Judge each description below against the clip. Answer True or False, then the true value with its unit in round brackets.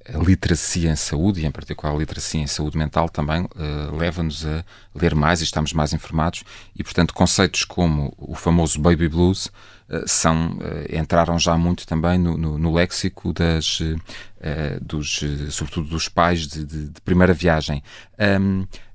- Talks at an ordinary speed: True (170 wpm)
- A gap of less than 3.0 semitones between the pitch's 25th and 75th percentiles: True (2.5 semitones)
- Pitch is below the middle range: True (85 Hz)